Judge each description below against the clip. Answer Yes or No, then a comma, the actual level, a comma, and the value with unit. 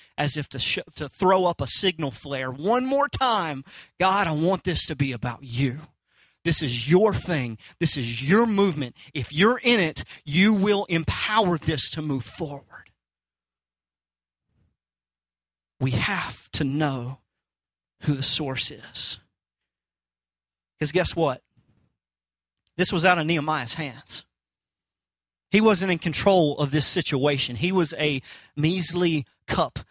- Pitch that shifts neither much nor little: No, wide, 7.7 semitones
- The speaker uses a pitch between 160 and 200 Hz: No, medium, 145 Hz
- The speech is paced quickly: No, average, 140 wpm